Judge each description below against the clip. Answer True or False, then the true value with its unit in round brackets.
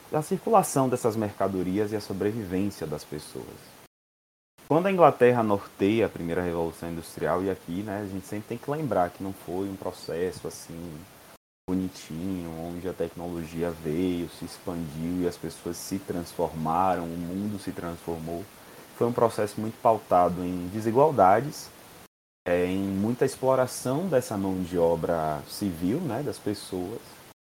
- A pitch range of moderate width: True (3.7 semitones)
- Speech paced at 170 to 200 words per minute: False (145 wpm)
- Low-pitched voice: True (90 Hz)